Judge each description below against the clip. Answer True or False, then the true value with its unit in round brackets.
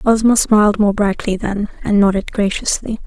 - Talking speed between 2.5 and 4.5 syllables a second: False (5.1 syllables/s)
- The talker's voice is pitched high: True (205 Hz)